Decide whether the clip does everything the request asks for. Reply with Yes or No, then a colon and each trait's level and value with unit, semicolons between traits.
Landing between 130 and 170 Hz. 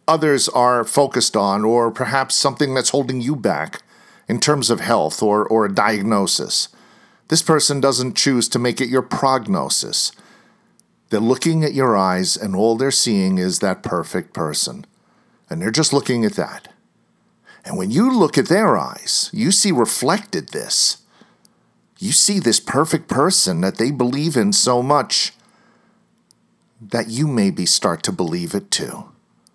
Yes: low, 135 Hz